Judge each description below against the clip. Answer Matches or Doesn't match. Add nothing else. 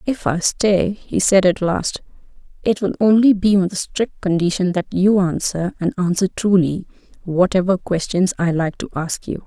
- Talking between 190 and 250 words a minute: Doesn't match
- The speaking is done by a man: Doesn't match